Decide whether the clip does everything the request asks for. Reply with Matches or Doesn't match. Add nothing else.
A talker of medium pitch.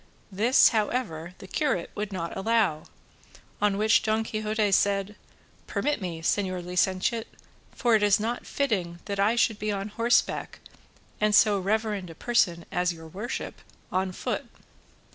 Doesn't match